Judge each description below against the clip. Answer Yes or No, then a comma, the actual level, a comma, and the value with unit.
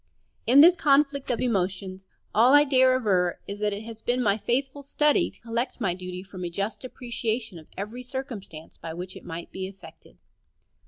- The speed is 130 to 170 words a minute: No, average, 190 wpm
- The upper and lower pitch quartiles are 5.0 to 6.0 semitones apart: Yes, wide, 5.4 semitones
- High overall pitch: Yes, high, 225 Hz